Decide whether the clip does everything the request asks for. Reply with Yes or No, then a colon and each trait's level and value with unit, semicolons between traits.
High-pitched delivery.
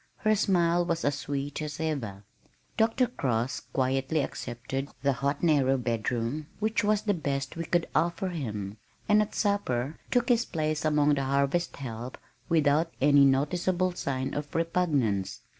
No: medium, 145 Hz